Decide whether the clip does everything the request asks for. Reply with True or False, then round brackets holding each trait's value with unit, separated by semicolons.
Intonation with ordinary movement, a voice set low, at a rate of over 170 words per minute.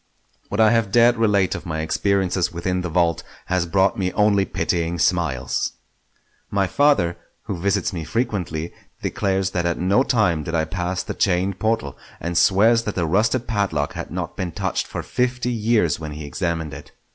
True (3.9 semitones; 95 Hz; 180 wpm)